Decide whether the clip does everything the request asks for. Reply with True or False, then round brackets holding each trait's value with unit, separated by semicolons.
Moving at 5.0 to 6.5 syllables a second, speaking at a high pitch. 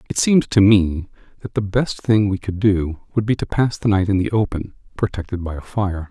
False (5.3 syllables/s; 100 Hz)